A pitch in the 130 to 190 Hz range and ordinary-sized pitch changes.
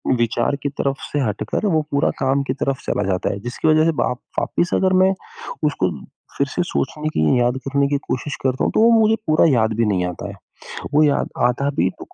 Yes: medium, 140 Hz; average, 4.1 semitones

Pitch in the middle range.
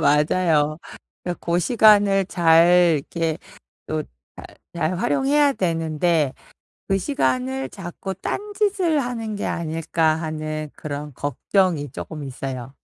Yes: medium, 165 Hz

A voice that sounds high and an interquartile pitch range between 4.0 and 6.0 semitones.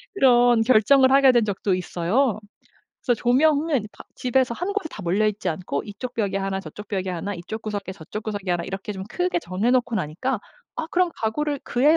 Yes: high, 220 Hz; average, 5.3 semitones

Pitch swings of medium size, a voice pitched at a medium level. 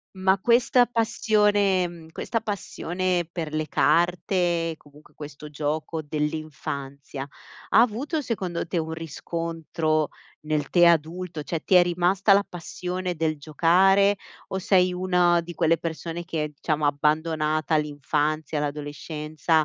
Yes: average, 3.0 semitones; medium, 165 Hz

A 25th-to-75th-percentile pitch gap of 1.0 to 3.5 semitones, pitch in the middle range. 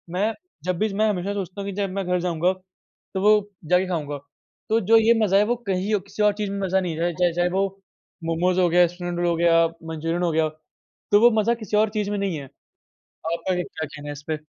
Yes: average, 3.2 semitones; medium, 180 Hz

